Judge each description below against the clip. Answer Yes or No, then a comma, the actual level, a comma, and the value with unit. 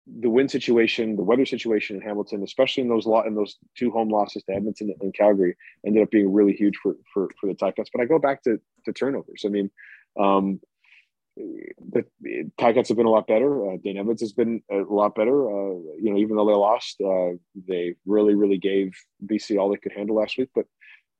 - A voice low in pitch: Yes, low, 105 Hz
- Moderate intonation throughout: No, narrow, 2.2 semitones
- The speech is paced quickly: Yes, fast, 220 wpm